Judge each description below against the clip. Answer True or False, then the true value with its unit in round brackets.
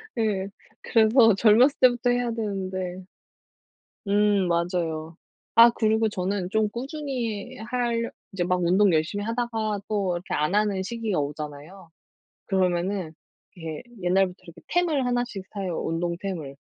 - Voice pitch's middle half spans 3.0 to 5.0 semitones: True (4.4 semitones)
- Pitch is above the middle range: True (200 Hz)